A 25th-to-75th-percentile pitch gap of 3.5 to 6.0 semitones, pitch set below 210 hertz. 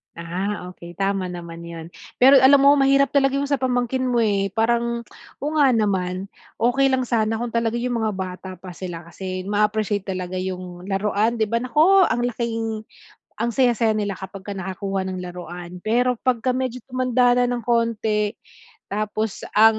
No: average, 4.6 semitones; high, 220 Hz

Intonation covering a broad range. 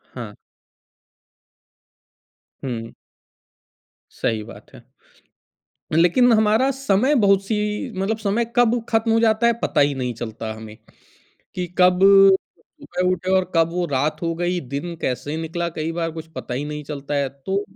Yes: wide, 6.6 semitones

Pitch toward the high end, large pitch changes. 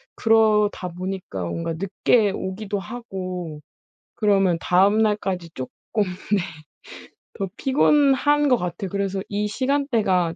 No: high, 195 Hz; average, 3.5 semitones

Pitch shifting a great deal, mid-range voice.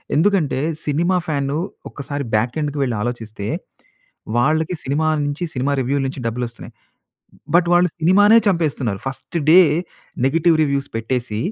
No: average, 4.7 semitones; medium, 145 Hz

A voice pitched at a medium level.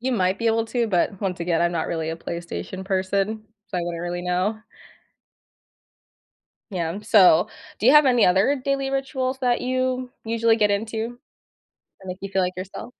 No: high, 205 Hz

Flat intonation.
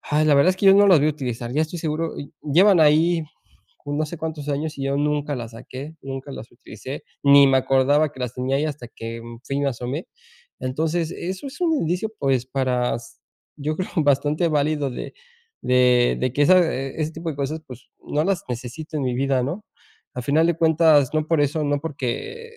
No: average, 3.5 semitones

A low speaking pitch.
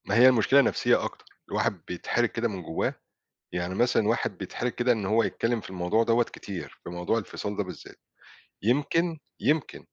Yes: low, 115 Hz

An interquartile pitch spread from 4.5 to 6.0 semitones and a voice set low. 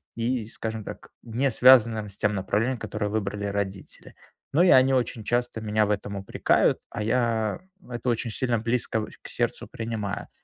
No: narrow, 2.5 semitones; low, 110 Hz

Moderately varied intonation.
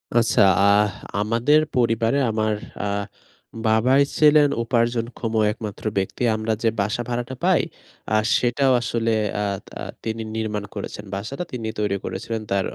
No: narrow, 2.2 semitones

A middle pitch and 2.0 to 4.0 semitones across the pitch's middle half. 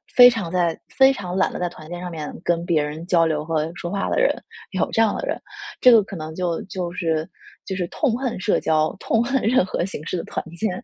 No: medium, 180 Hz; average, 4.9 semitones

